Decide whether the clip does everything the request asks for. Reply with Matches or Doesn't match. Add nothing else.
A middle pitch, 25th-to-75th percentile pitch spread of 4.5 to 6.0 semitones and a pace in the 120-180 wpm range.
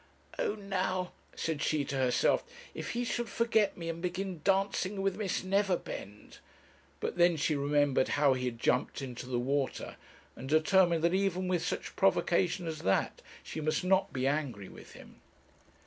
Matches